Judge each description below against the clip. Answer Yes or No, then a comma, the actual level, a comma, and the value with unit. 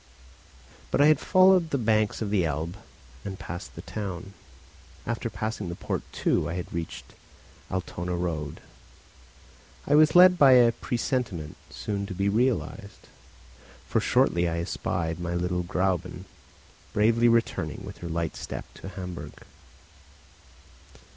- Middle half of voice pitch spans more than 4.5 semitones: Yes, average, 5.1 semitones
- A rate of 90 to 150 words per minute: Yes, average, 140 wpm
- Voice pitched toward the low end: Yes, very low, 95 Hz